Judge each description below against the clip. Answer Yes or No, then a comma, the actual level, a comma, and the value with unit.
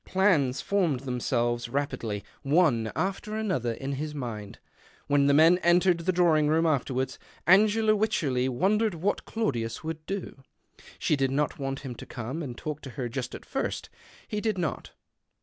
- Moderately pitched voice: Yes, medium, 150 Hz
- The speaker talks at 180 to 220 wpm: No, average, 165 wpm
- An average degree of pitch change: No, wide, 6.0 semitones